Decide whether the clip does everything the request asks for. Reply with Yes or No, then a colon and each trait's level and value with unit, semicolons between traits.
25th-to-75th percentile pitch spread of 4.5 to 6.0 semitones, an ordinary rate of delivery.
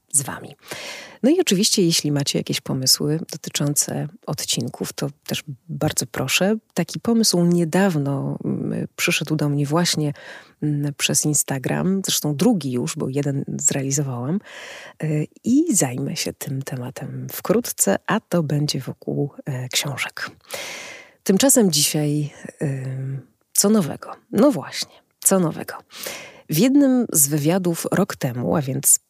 Yes: average, 4.9 semitones; average, 120 wpm